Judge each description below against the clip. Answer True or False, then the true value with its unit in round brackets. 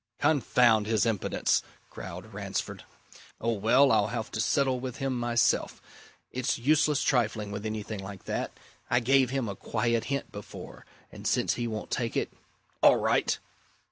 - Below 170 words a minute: True (155 wpm)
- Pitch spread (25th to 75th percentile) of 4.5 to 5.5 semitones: False (3.2 semitones)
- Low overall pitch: True (120 Hz)